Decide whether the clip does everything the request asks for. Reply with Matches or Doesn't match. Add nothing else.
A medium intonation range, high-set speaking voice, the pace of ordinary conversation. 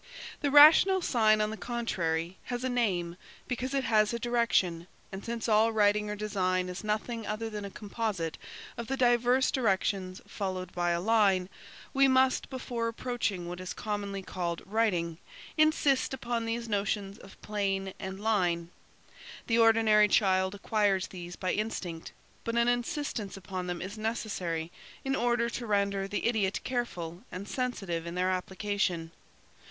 Matches